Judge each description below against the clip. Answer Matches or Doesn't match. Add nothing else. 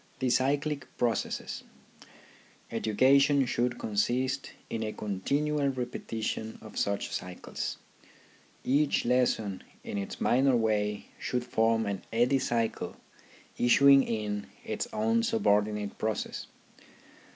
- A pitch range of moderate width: Matches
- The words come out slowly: Matches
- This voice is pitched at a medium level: Doesn't match